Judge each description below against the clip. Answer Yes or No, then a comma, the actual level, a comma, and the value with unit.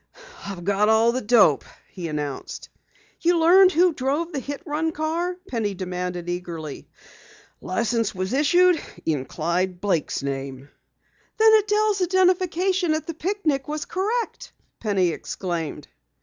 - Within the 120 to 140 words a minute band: Yes, slow, 135 wpm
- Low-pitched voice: No, very high, 255 Hz